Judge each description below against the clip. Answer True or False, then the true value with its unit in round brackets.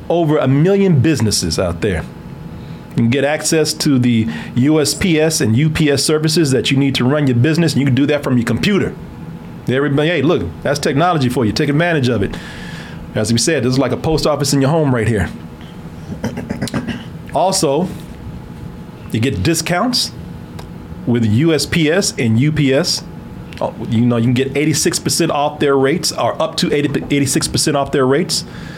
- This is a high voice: False (140 Hz)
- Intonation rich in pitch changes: False (4.2 semitones)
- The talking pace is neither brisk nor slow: True (170 wpm)